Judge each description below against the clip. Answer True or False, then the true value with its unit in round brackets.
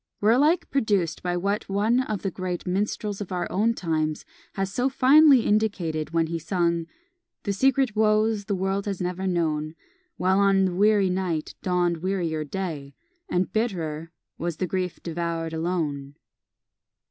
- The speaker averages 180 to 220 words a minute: False (155 wpm)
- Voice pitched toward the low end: False (185 Hz)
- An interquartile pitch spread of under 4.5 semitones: True (3.7 semitones)